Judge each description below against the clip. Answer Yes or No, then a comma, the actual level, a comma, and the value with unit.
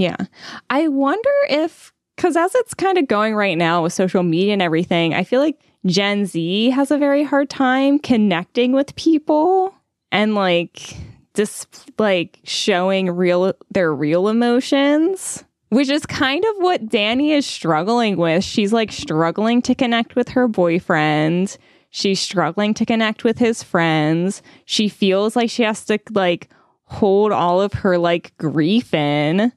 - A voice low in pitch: No, high, 215 Hz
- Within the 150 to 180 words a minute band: Yes, average, 160 wpm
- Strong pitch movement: Yes, wide, 6.8 semitones